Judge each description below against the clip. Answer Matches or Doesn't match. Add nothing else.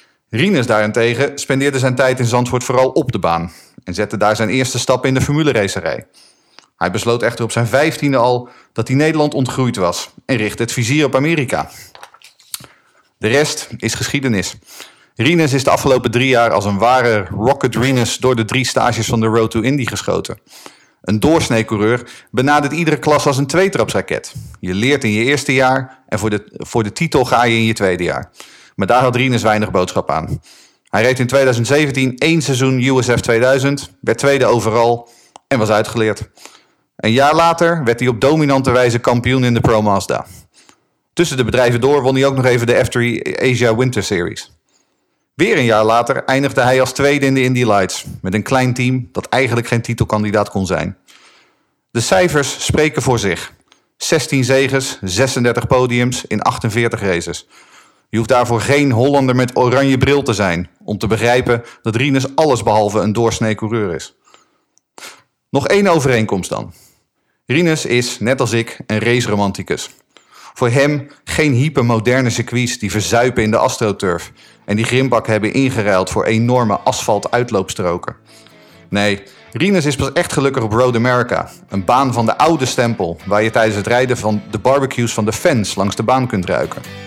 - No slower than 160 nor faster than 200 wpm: Matches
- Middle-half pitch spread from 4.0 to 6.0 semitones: Doesn't match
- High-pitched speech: Doesn't match